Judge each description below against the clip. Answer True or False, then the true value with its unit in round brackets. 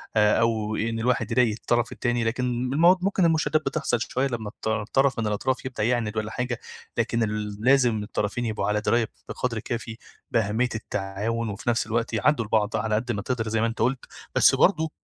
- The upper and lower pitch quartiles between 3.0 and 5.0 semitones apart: False (2.5 semitones)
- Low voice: True (115 Hz)